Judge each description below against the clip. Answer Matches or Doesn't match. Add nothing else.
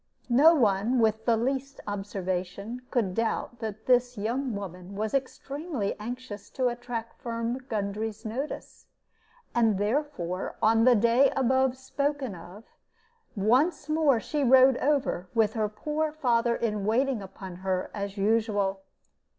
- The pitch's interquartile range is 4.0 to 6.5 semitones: Matches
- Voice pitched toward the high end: Matches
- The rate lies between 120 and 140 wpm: Matches